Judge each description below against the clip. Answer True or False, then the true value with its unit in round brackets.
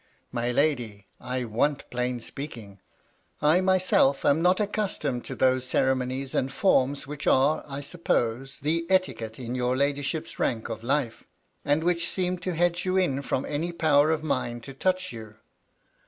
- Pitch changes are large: False (5.0 semitones)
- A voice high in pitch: False (140 Hz)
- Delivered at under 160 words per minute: False (165 wpm)